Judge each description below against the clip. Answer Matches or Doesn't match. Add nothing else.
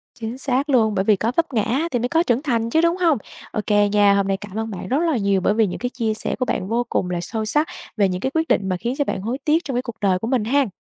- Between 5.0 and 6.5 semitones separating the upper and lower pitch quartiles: Doesn't match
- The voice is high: Matches